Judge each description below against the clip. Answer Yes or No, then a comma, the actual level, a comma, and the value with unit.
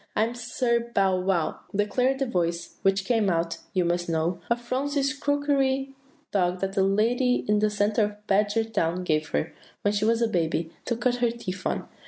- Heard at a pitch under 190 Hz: No, high, 210 Hz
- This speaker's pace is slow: No, average, 190 wpm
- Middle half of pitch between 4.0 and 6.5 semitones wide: Yes, average, 4.8 semitones